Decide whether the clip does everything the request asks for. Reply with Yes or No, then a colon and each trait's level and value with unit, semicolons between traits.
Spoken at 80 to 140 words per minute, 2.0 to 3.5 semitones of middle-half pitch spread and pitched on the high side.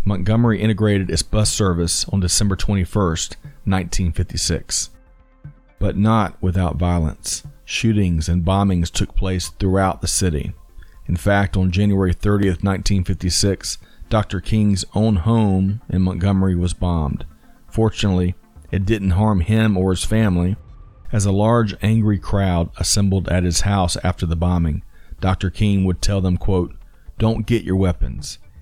No: slow, 135 wpm; average, 2.7 semitones; very low, 95 Hz